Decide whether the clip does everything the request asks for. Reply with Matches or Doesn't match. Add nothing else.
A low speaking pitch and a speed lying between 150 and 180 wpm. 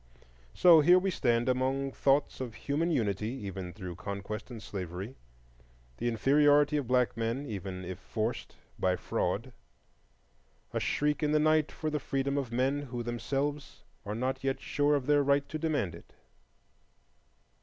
Matches